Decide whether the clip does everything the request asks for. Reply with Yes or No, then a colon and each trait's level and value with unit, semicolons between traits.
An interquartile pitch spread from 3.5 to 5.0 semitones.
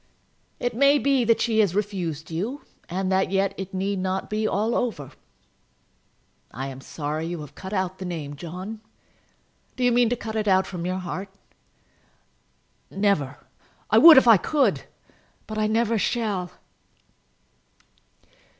Yes: average, 3.9 semitones